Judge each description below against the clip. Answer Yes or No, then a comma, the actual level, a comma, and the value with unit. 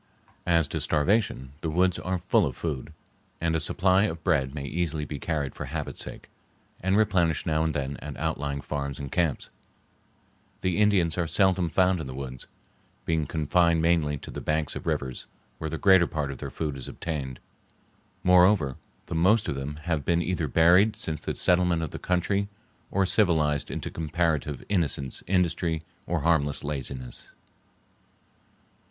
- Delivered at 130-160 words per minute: No, average, 170 wpm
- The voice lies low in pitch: Yes, very low, 80 Hz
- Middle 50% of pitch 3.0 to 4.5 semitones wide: Yes, average, 3.7 semitones